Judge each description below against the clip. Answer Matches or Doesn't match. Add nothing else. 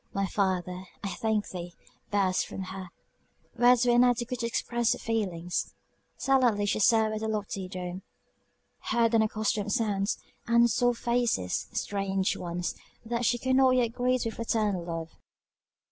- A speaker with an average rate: Matches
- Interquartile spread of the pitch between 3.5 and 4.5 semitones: Matches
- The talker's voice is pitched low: Doesn't match